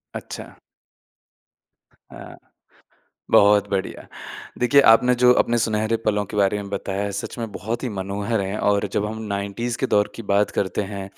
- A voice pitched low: Yes, low, 105 Hz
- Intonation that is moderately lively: No, narrow, 2.2 semitones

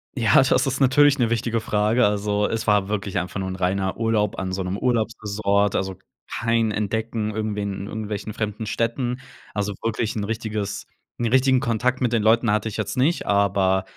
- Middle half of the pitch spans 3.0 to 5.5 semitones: No, narrow, 2.5 semitones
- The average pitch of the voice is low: Yes, low, 110 Hz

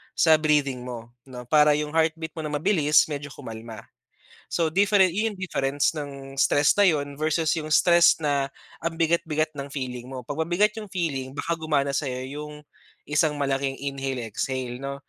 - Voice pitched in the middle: Yes, medium, 150 Hz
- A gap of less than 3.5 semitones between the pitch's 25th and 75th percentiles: Yes, average, 2.9 semitones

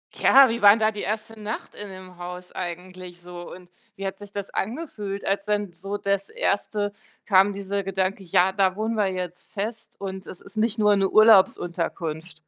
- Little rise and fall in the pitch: Yes, narrow, 2.2 semitones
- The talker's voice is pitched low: No, high, 195 Hz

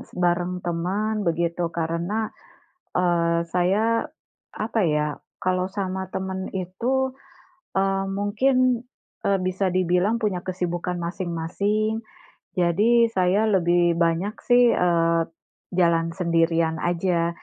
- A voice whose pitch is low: No, medium, 180 Hz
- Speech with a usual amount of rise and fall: Yes, average, 3.1 semitones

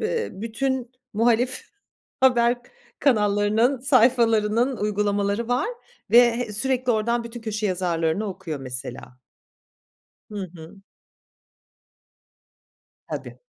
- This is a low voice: No, high, 225 Hz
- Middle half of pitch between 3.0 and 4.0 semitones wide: Yes, average, 3.3 semitones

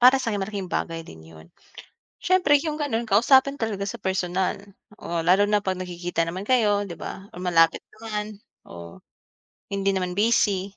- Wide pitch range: No, average, 3.8 semitones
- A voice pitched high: Yes, high, 195 Hz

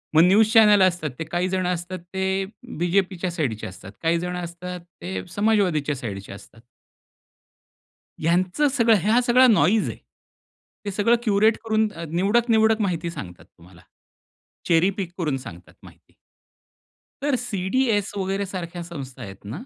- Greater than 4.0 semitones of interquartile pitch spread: Yes, average, 4.4 semitones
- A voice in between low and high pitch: Yes, medium, 180 Hz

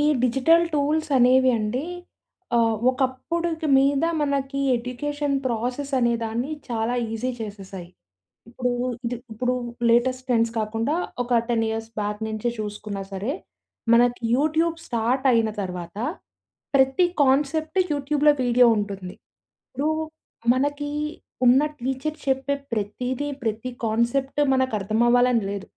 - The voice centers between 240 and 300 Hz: Yes, very high, 250 Hz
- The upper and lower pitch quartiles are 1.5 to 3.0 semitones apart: No, average, 3.8 semitones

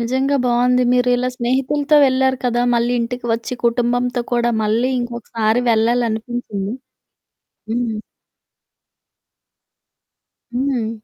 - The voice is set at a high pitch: Yes, high, 245 Hz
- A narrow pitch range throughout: Yes, narrow, 1.4 semitones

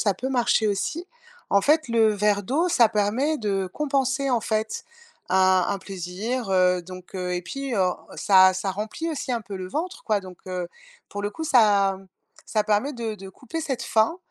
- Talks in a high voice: Yes, high, 210 Hz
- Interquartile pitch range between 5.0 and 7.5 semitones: Yes, average, 5.3 semitones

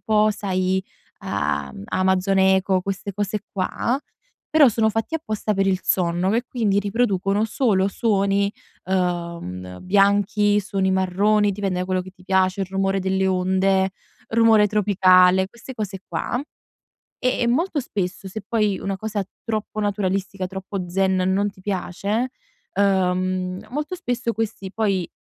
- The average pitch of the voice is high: Yes, high, 195 Hz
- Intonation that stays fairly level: Yes, narrow, 2.2 semitones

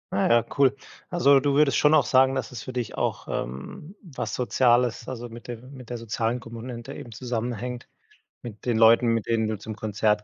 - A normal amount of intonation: No, narrow, 2.3 semitones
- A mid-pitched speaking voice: No, low, 120 Hz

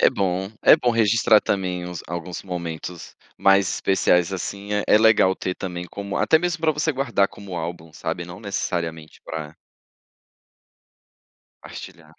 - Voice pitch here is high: No, very low, 95 Hz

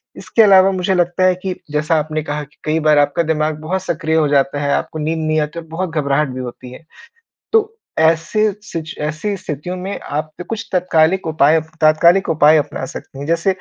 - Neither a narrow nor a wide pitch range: Yes, average, 3.3 semitones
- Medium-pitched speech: Yes, medium, 160 Hz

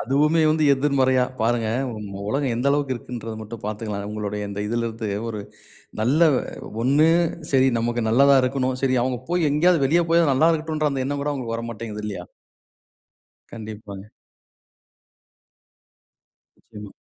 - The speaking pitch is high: No, low, 125 Hz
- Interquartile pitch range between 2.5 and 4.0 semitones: No, average, 4.5 semitones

